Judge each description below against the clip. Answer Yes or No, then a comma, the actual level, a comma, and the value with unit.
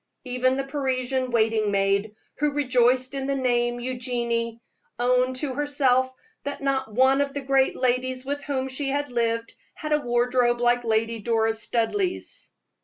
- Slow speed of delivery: No, average, 160 wpm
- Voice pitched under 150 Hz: No, very high, 255 Hz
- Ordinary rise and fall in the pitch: No, narrow, 2.3 semitones